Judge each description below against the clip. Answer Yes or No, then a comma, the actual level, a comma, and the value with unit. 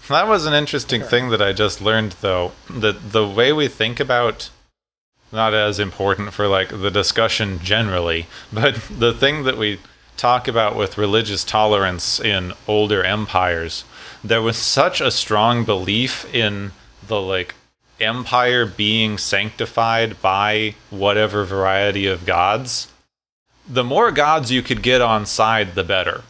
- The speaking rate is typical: Yes, average, 145 wpm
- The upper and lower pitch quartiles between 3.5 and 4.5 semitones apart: No, narrow, 2.4 semitones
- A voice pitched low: Yes, low, 110 Hz